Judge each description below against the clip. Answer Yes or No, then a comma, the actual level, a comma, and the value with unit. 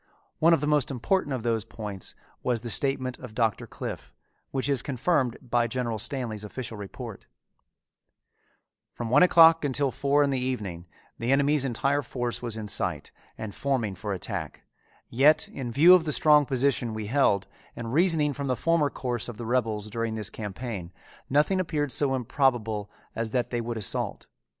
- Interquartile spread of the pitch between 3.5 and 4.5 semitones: Yes, average, 4.1 semitones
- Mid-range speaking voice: No, low, 125 Hz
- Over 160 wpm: Yes, average, 175 wpm